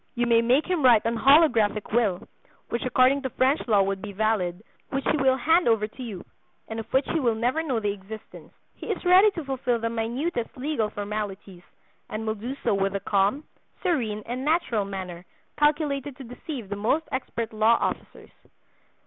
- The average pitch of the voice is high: Yes, high, 235 Hz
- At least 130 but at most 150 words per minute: No, average, 190 wpm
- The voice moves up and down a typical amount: Yes, average, 4.5 semitones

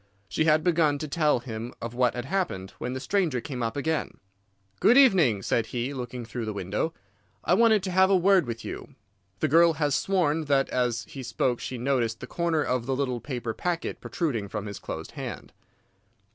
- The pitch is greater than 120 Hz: Yes, low, 135 Hz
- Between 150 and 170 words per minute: No, average, 200 wpm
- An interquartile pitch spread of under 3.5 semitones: No, wide, 5.6 semitones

